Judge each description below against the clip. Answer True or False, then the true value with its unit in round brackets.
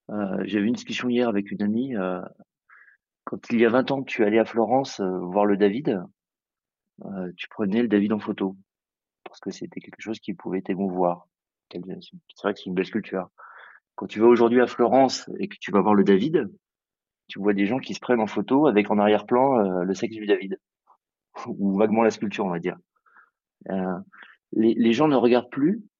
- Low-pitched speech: True (105 Hz)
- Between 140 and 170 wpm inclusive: False (210 wpm)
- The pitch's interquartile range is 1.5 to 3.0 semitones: False (3.8 semitones)